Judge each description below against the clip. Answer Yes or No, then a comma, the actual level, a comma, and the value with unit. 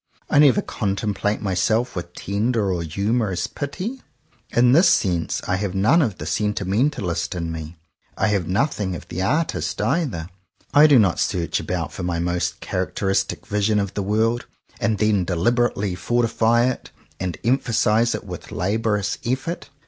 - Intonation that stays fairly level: No, average, 4.5 semitones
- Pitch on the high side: No, low, 105 Hz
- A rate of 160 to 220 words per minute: No, average, 150 wpm